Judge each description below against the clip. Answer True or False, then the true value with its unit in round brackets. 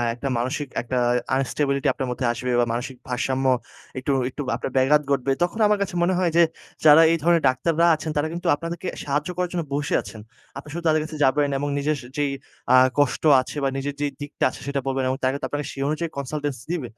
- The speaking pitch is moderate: True (145 Hz)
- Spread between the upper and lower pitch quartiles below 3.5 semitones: True (3.0 semitones)